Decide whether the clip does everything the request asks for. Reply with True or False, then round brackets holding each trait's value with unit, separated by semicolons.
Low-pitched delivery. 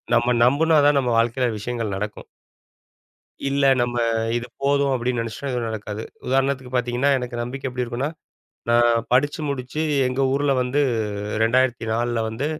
True (125 Hz)